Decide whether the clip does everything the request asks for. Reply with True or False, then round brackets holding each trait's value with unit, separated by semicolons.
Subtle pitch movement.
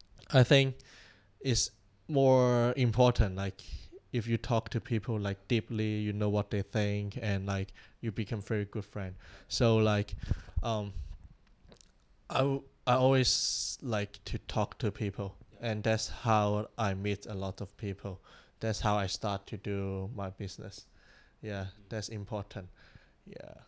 True (2.3 semitones)